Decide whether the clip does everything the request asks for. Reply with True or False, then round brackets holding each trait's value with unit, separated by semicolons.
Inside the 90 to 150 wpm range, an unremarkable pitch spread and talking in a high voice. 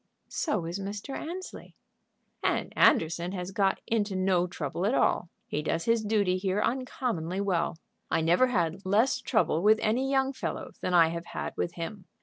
False (170 wpm; 4.3 semitones; 195 Hz)